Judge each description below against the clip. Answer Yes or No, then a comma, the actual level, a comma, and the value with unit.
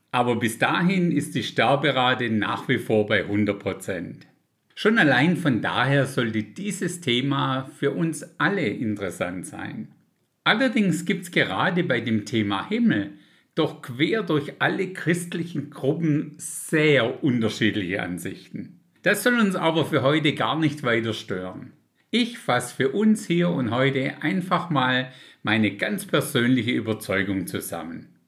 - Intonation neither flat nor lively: No, wide, 6.8 semitones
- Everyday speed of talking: Yes, average, 135 wpm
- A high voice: No, medium, 140 Hz